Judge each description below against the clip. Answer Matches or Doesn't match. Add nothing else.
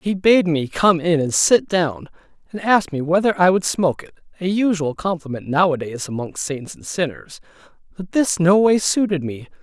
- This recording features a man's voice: Matches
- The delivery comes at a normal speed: Matches